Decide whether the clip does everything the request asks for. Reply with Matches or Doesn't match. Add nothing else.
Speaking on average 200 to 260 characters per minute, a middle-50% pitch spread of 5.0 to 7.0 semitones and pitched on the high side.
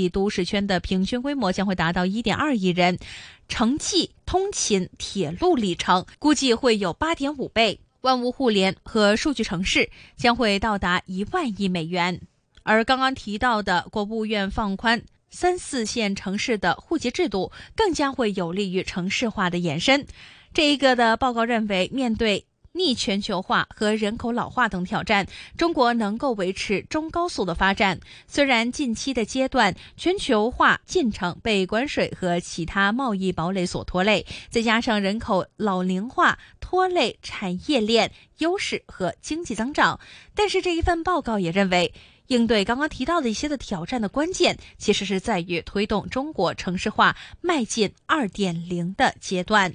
Matches